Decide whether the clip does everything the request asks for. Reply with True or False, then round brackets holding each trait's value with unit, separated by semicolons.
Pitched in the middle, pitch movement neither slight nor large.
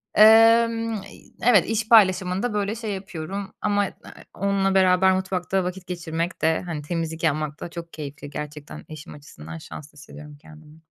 True (180 Hz; 4.5 semitones)